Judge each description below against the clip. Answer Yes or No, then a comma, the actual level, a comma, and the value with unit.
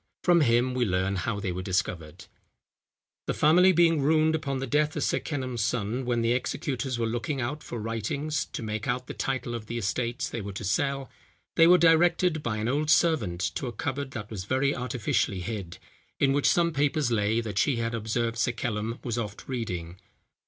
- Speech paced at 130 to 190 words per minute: No, average, 200 wpm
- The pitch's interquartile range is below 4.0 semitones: No, average, 4.9 semitones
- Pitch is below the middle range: Yes, low, 120 Hz